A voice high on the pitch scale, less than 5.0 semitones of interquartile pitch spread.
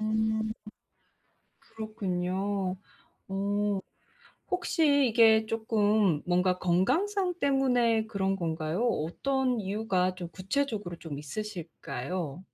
Yes: high, 210 Hz; average, 4.0 semitones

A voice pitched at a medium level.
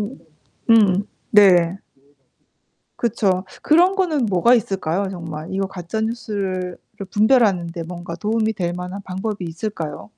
No: high, 195 Hz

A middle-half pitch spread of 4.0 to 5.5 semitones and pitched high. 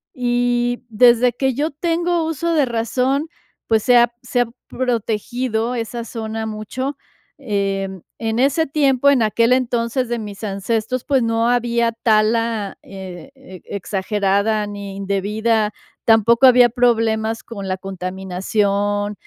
No: average, 3.2 semitones; high, 230 Hz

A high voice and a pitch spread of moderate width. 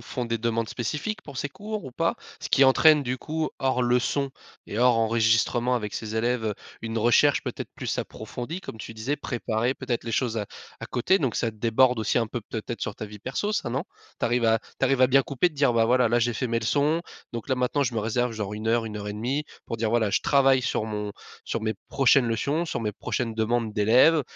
No: low, 120 Hz; average, 3.0 semitones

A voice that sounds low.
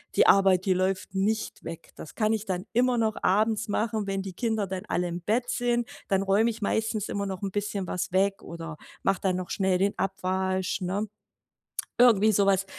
No: high, 195 Hz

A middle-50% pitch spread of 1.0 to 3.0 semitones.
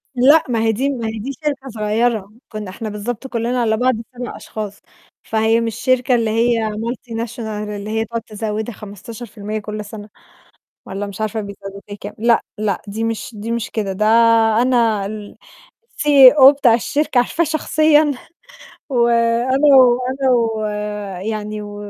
Yes: average, 2.7 semitones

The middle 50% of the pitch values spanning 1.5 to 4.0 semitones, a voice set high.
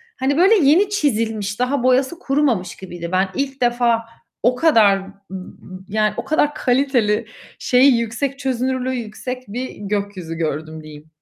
No: average, 5.0 semitones; high, 240 Hz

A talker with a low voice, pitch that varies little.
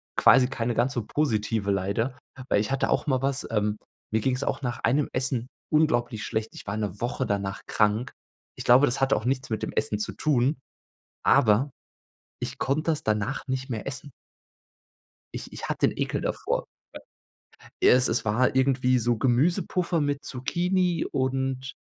No: low, 125 Hz; average, 3.6 semitones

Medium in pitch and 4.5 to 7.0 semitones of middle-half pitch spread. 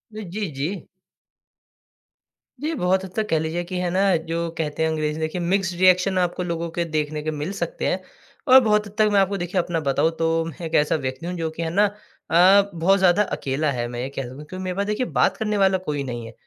No: medium, 175 Hz; average, 3.9 semitones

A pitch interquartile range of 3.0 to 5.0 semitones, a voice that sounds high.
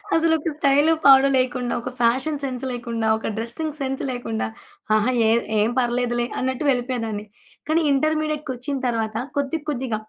Yes: average, 3.3 semitones; very high, 255 Hz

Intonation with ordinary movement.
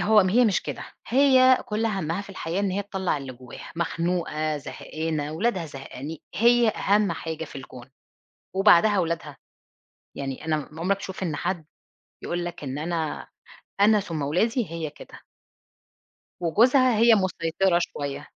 Yes: average, 5.0 semitones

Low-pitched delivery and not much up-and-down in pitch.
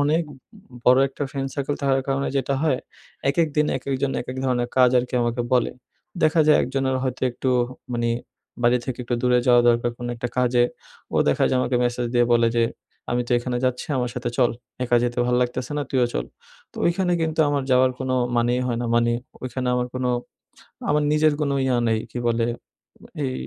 Yes: low, 125 Hz; narrow, 1.9 semitones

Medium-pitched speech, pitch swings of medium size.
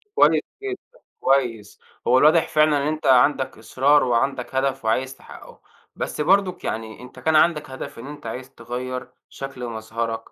No: low, 130 Hz; average, 3.6 semitones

